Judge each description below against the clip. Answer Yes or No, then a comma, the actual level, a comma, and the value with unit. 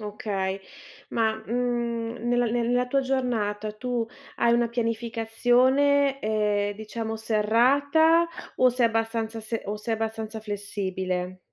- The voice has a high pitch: Yes, high, 225 Hz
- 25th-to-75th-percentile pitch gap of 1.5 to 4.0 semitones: Yes, narrow, 2.4 semitones